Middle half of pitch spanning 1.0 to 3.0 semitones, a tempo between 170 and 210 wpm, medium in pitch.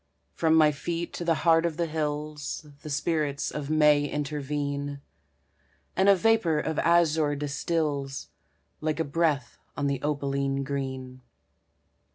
No: narrow, 2.4 semitones; slow, 135 wpm; medium, 150 Hz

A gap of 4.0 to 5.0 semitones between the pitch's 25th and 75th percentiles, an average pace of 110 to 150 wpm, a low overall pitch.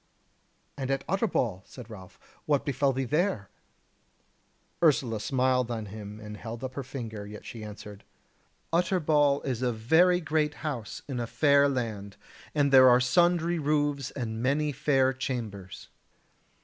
Yes: average, 4.7 semitones; average, 145 wpm; low, 130 Hz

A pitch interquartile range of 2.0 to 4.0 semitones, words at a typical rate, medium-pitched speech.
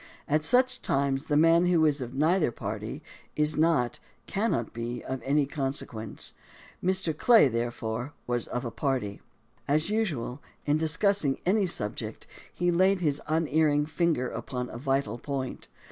No: average, 5.1 semitones; average, 150 wpm; medium, 145 Hz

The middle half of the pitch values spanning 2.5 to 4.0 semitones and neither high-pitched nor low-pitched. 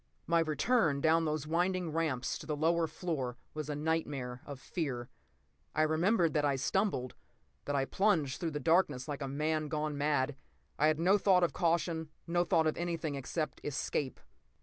Yes: average, 2.8 semitones; medium, 155 Hz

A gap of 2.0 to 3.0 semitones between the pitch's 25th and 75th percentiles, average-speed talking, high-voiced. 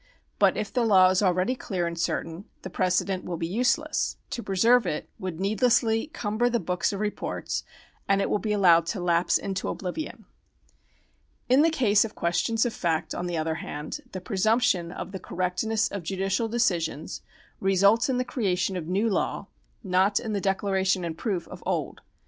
No: average, 3.8 semitones; average, 185 wpm; high, 195 Hz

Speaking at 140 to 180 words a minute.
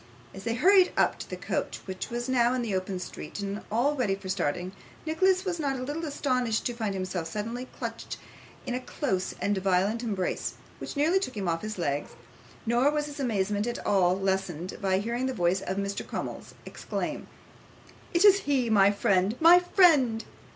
No: average, 190 wpm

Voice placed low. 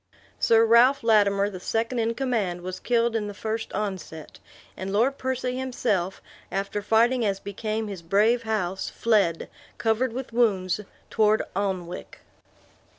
No: high, 215 Hz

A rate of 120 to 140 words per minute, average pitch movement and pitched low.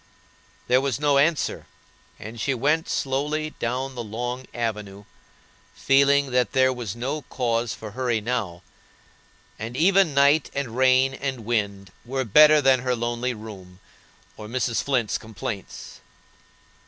Yes: slow, 135 wpm; average, 3.5 semitones; low, 125 Hz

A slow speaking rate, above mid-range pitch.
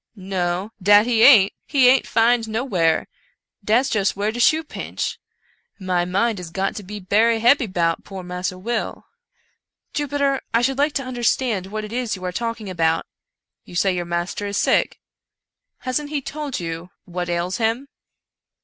No: average, 185 wpm; high, 210 Hz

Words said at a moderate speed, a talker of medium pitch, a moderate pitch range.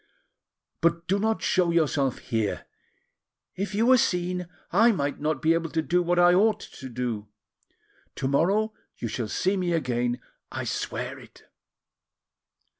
No: average, 150 wpm; medium, 170 Hz; wide, 5.9 semitones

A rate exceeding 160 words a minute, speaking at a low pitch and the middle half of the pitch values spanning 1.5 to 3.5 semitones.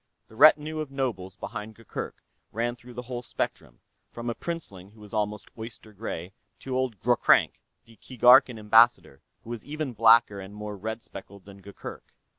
Yes: average, 170 wpm; low, 115 Hz; average, 3.2 semitones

